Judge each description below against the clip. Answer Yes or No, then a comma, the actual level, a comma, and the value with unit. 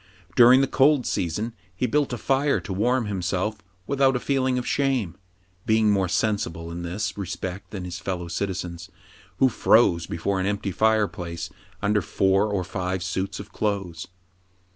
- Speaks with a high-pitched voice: No, low, 100 Hz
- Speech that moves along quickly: No, average, 165 wpm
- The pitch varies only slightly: No, average, 4.7 semitones